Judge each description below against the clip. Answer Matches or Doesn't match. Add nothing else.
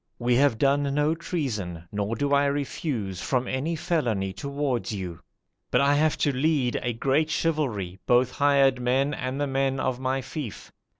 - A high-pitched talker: Doesn't match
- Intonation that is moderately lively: Matches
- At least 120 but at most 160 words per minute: Doesn't match